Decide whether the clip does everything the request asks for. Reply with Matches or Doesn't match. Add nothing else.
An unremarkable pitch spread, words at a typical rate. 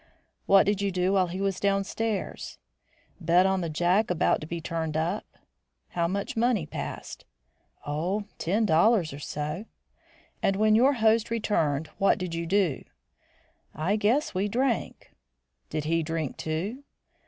Matches